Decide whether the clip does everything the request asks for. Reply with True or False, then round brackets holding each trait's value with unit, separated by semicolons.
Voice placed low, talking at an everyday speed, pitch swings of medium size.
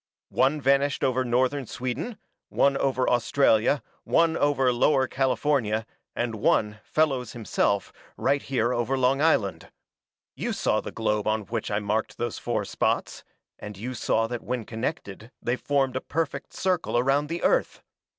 True (130 Hz; 150 wpm; 3.7 semitones)